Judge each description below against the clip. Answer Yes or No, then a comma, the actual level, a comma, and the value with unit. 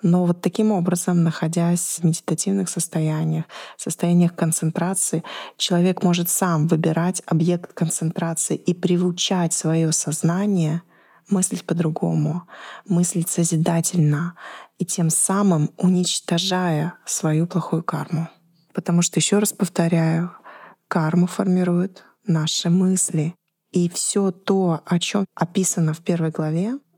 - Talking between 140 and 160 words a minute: No, slow, 110 wpm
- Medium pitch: Yes, medium, 175 Hz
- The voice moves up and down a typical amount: No, narrow, 1.9 semitones